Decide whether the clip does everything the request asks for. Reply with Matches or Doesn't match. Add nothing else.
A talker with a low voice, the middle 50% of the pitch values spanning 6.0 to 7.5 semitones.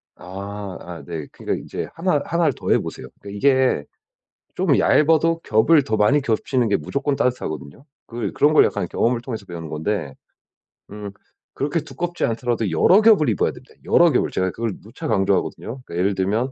Matches